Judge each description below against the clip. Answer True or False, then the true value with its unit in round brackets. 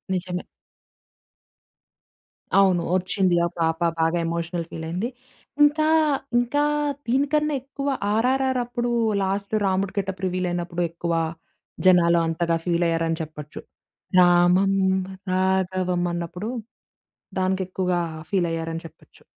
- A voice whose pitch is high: False (180 Hz)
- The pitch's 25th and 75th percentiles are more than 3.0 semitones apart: False (2.6 semitones)